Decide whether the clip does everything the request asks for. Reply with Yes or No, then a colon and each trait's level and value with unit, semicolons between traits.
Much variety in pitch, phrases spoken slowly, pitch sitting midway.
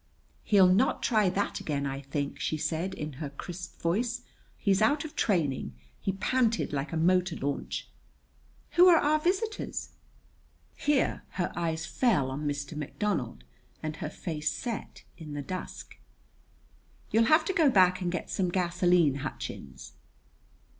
No: wide, 6.8 semitones; average, 145 wpm; medium, 180 Hz